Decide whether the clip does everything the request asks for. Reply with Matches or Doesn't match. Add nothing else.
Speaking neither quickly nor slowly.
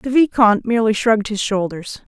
Matches